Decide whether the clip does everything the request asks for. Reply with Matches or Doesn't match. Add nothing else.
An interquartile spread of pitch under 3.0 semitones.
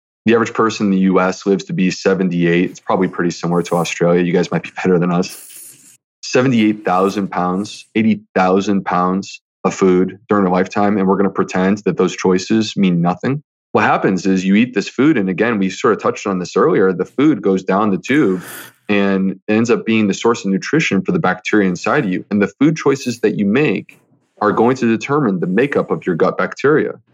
Matches